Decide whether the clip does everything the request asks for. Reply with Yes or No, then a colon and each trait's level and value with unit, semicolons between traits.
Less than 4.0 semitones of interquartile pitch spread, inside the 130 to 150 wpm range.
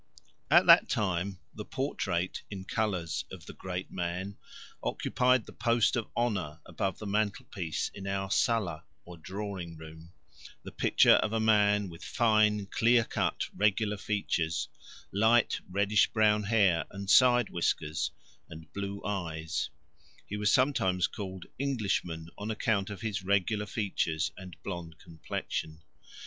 Yes: average, 3.5 semitones; slow, 135 wpm